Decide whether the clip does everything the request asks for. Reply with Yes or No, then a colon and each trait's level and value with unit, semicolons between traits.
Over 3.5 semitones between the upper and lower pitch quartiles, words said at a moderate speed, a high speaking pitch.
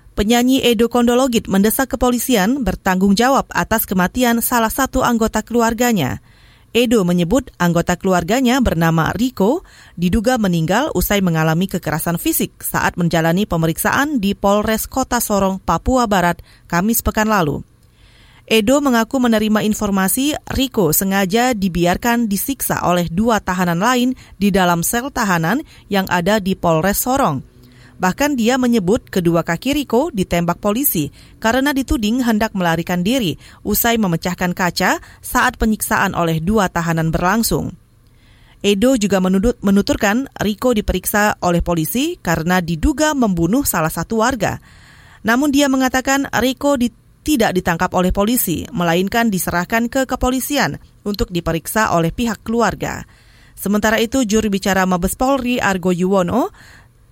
Yes: wide, 5.5 semitones; average, 125 wpm; high, 205 Hz